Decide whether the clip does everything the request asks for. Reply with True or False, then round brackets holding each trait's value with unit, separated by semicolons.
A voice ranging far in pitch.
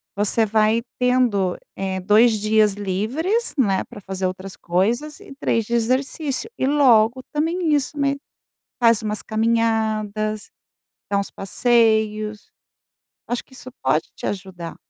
False (3.7 semitones)